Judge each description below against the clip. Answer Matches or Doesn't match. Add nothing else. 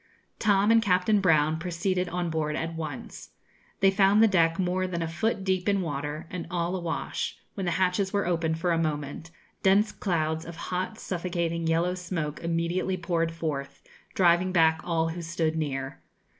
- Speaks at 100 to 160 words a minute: Doesn't match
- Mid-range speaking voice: Matches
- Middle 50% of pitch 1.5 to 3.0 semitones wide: Matches